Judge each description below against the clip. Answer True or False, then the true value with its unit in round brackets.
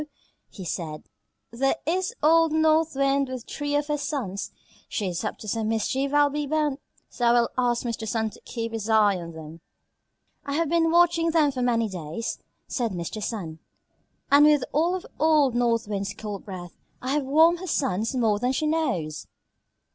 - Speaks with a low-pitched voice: False (250 Hz)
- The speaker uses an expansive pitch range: True (6.0 semitones)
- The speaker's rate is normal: True (185 wpm)